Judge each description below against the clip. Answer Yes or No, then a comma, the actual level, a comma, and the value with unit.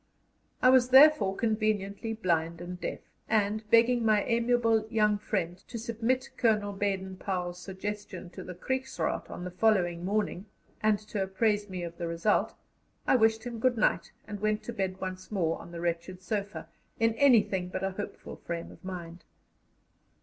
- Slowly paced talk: No, average, 165 wpm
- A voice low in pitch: No, high, 205 Hz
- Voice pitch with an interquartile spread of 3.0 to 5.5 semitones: Yes, average, 3.6 semitones